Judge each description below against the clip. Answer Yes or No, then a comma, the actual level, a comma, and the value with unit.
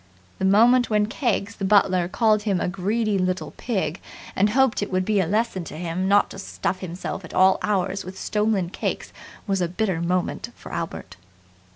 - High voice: Yes, high, 195 Hz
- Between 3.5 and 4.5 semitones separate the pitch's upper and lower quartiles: No, narrow, 2.5 semitones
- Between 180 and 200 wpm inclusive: Yes, average, 190 wpm